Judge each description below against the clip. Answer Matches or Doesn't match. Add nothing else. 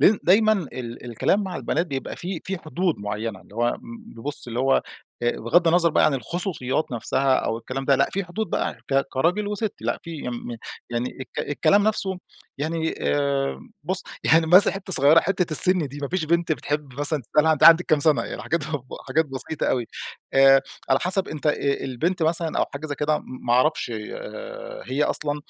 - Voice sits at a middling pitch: Matches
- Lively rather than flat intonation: Doesn't match